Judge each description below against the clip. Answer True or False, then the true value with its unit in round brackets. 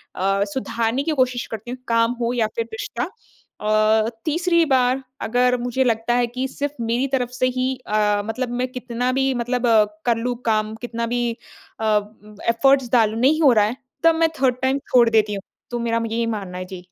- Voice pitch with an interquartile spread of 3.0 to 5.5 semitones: False (2.4 semitones)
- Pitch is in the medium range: False (240 Hz)